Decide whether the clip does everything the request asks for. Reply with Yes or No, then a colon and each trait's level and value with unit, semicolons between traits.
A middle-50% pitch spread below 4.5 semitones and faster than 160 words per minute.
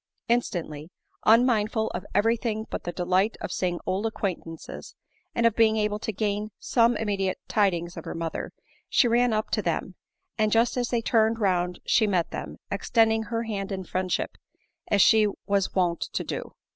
Yes: average, 3.4 semitones; average, 175 wpm